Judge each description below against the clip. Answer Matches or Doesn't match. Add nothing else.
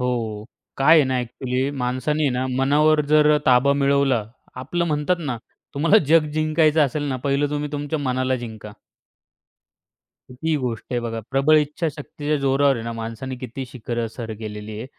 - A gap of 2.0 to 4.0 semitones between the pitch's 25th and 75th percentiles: Matches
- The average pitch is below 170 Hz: Matches